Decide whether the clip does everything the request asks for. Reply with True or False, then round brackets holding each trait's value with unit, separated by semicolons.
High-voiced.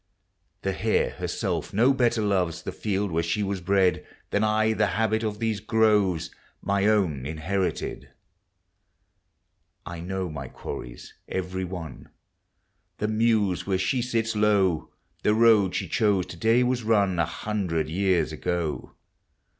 False (100 Hz)